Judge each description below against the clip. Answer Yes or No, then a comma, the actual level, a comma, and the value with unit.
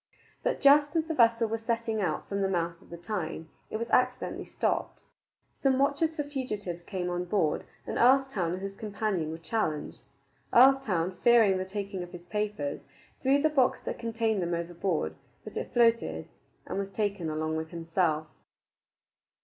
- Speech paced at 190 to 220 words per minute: No, average, 170 wpm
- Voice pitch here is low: No, high, 200 Hz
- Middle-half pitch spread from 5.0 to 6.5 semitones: Yes, wide, 5.6 semitones